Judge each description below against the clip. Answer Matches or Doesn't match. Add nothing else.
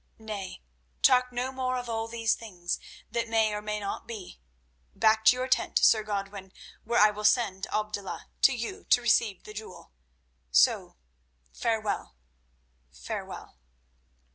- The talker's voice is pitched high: Matches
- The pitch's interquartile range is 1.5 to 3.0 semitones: Matches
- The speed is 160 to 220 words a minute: Doesn't match